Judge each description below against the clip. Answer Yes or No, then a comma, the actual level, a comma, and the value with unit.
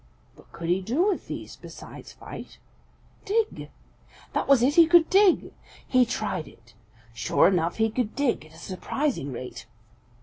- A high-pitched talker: Yes, high, 240 Hz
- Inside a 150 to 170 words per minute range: Yes, average, 160 wpm